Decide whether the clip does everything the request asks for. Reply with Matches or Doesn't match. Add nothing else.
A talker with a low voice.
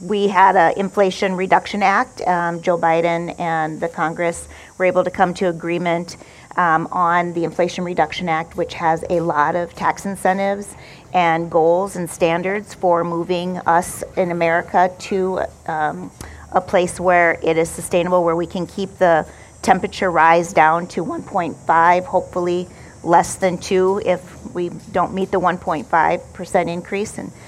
Doesn't match